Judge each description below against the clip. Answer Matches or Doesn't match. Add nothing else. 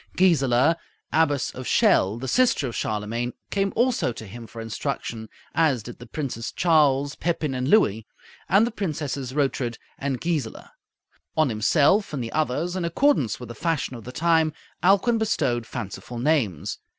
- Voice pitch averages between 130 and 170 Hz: Matches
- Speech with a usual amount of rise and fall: Doesn't match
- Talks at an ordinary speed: Matches